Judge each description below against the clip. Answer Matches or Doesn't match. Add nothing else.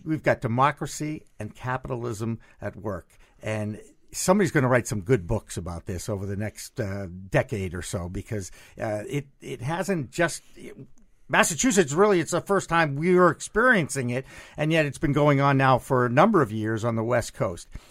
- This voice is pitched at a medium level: Doesn't match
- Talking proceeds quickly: Doesn't match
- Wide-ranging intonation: Matches